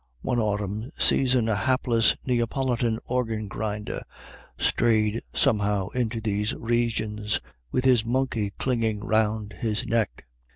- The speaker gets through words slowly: Yes, slow, 115 wpm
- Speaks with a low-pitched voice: Yes, low, 110 Hz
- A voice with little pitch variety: Yes, narrow, 2.2 semitones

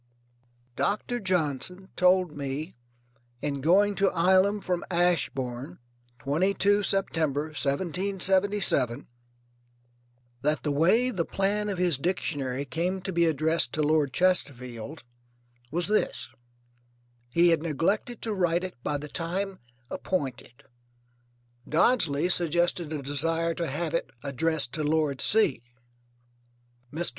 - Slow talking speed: Yes, slow, 115 wpm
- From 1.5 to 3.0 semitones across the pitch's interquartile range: No, average, 4.4 semitones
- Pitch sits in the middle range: Yes, medium, 165 Hz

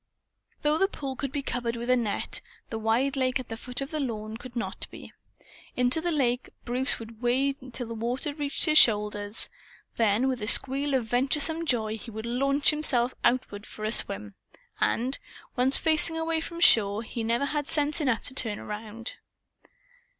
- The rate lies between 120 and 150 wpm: No, average, 185 wpm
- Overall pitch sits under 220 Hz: No, very high, 250 Hz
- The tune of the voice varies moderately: Yes, average, 3.7 semitones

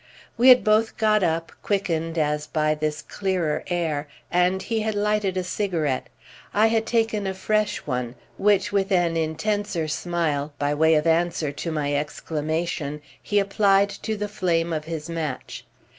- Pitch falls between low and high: Yes, medium, 170 Hz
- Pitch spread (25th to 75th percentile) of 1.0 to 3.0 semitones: No, average, 4.9 semitones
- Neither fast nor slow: Yes, average, 160 wpm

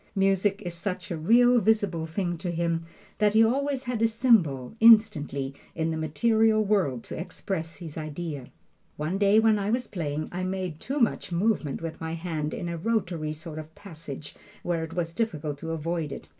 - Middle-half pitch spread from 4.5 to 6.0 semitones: Yes, average, 5.1 semitones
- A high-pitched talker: No, medium, 175 Hz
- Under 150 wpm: No, average, 190 wpm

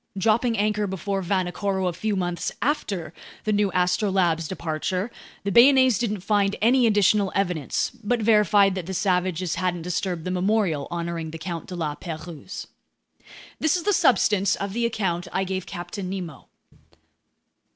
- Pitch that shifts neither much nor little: Yes, average, 3.1 semitones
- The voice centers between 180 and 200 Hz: Yes, high, 190 Hz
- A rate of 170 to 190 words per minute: No, average, 150 wpm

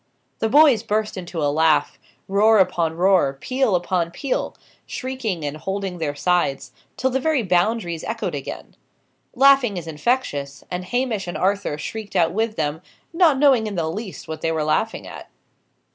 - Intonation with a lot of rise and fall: Yes, wide, 6.1 semitones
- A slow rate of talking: No, average, 165 wpm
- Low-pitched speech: No, high, 190 Hz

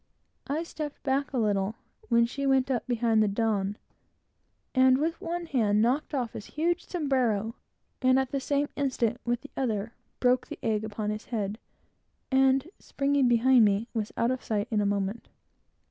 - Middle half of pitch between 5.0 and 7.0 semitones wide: No, average, 3.9 semitones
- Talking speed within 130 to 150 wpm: No, average, 175 wpm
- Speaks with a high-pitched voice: Yes, high, 245 Hz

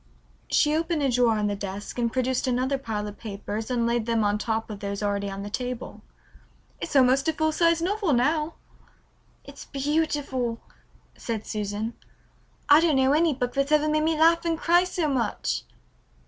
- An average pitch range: No, wide, 5.8 semitones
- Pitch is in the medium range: No, very high, 255 Hz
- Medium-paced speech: Yes, average, 180 wpm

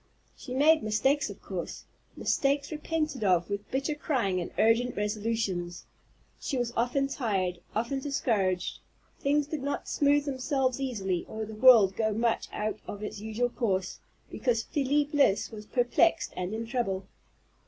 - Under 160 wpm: Yes, average, 150 wpm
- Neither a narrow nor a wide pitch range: Yes, average, 4.9 semitones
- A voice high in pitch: Yes, high, 235 Hz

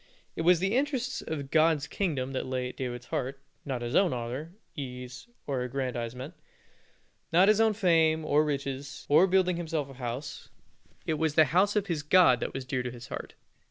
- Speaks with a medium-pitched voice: Yes, medium, 145 Hz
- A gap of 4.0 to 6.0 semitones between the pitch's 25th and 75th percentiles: Yes, average, 5.2 semitones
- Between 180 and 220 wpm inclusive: Yes, average, 190 wpm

